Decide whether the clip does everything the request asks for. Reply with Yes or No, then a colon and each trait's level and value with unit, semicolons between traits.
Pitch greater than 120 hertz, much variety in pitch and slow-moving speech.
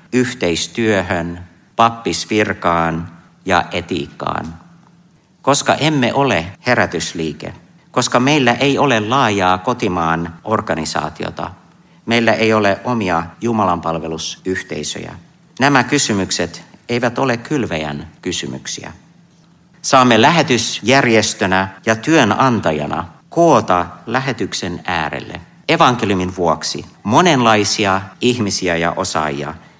No: low, 110 Hz; wide, 6.8 semitones; slow, 80 wpm